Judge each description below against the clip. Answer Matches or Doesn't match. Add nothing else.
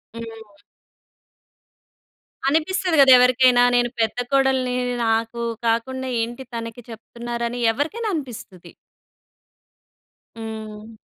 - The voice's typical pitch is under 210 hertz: Doesn't match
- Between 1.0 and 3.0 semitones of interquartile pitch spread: Matches